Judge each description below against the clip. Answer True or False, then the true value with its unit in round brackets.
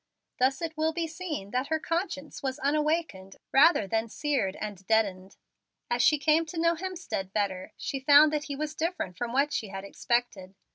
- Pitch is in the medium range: False (280 Hz)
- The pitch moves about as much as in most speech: False (7.0 semitones)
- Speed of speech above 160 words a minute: True (185 wpm)